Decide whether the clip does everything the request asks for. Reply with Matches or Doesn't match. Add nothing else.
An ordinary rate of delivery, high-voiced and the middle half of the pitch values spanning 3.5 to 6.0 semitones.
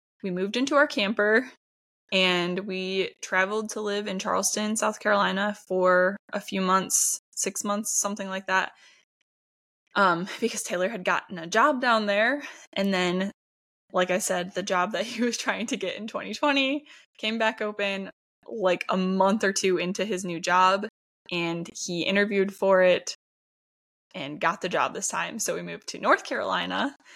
Doesn't match